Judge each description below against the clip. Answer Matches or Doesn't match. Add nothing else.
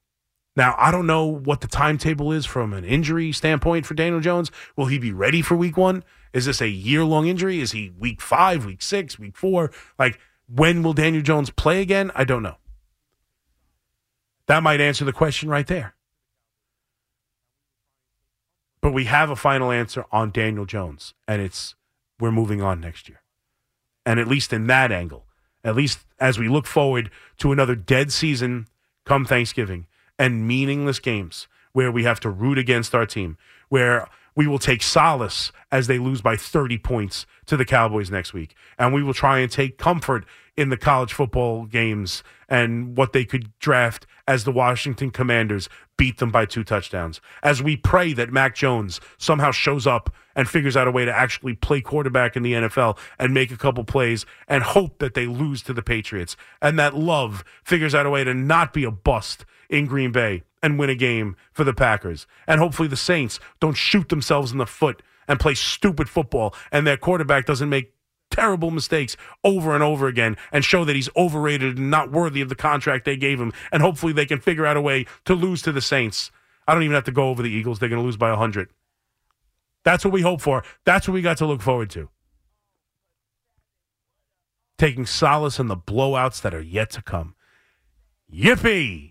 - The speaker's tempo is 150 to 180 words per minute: Doesn't match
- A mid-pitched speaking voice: Doesn't match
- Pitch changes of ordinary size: Matches